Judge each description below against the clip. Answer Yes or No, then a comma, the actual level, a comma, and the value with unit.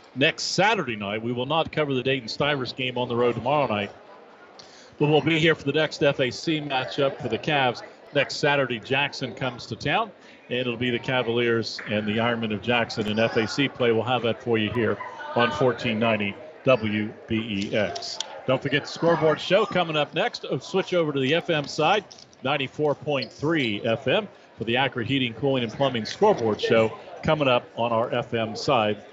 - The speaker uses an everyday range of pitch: Yes, average, 4.1 semitones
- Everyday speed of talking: Yes, average, 180 wpm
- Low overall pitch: Yes, low, 125 Hz